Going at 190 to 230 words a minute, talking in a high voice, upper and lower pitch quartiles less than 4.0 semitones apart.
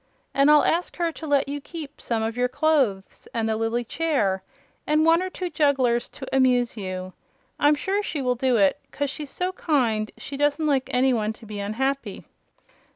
No: average, 195 wpm; very high, 270 Hz; average, 4.9 semitones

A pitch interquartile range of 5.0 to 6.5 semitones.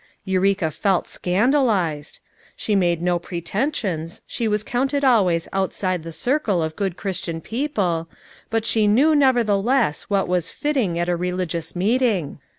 Yes: average, 5.3 semitones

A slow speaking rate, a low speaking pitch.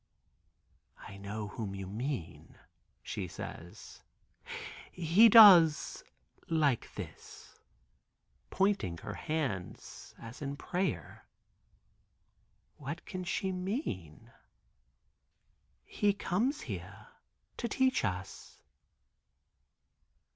No: slow, 80 wpm; medium, 155 Hz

